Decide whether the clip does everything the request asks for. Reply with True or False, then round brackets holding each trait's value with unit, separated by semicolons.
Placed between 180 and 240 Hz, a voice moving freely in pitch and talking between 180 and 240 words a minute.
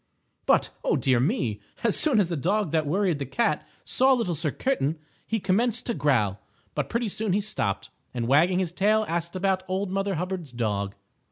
True (185 Hz; 6.6 semitones; 190 wpm)